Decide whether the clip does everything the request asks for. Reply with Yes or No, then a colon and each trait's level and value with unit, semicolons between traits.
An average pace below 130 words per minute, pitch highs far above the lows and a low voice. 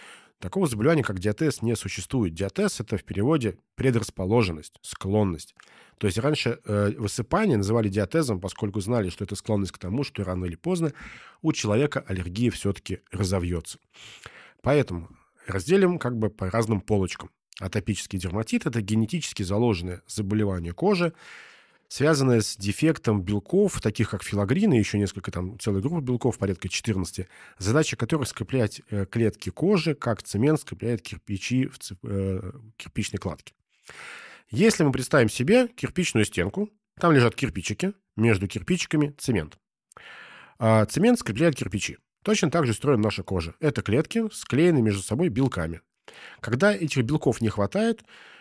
No: average, 135 wpm; wide, 6.3 semitones; low, 110 Hz